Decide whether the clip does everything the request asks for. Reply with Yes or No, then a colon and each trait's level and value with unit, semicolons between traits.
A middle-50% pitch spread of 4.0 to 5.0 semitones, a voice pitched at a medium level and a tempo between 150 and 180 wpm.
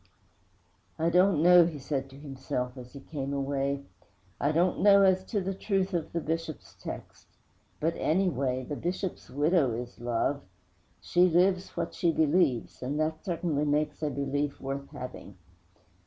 Yes: average, 4.4 semitones; medium, 150 Hz; average, 155 wpm